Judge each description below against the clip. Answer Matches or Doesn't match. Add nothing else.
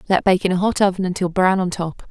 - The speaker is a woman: Matches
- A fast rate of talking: Matches